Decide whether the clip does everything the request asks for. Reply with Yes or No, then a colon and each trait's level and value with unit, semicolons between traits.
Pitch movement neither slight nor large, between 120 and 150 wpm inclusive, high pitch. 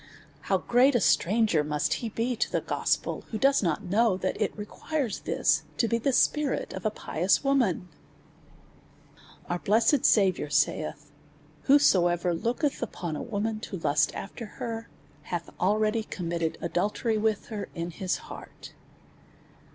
Yes: average, 5.0 semitones; average, 145 wpm; high, 210 Hz